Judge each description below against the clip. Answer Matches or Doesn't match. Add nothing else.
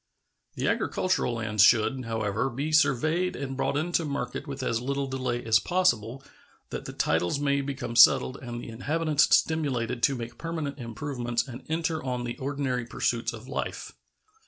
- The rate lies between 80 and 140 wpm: Doesn't match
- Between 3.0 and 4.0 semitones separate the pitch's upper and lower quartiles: Matches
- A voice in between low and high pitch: Doesn't match